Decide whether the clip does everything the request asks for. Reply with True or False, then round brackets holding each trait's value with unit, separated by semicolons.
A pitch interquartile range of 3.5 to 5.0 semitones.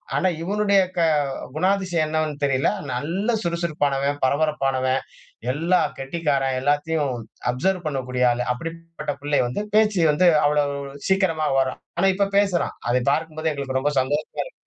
True (4.1 semitones)